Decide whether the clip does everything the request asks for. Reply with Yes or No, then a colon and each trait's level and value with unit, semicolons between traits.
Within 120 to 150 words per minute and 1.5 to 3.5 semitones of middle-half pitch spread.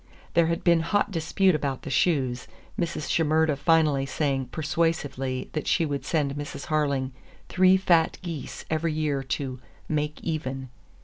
Yes: average, 145 wpm; average, 3.2 semitones